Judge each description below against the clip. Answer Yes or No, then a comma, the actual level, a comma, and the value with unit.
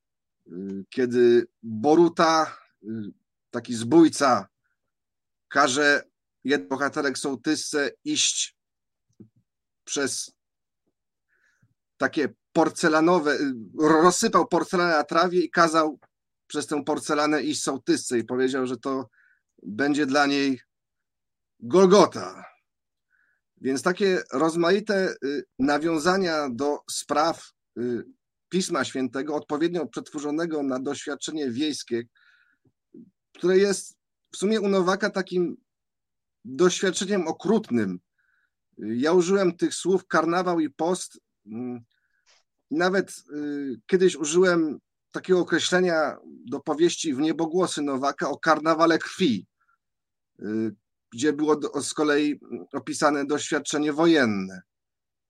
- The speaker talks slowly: Yes, slow, 85 wpm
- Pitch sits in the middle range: Yes, medium, 155 Hz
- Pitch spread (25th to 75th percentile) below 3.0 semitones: No, average, 4.6 semitones